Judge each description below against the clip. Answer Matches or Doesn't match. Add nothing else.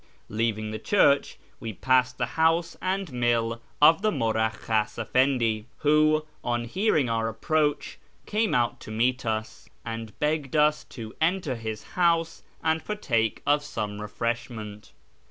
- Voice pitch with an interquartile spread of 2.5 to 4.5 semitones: Doesn't match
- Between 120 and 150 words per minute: Matches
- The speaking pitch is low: Matches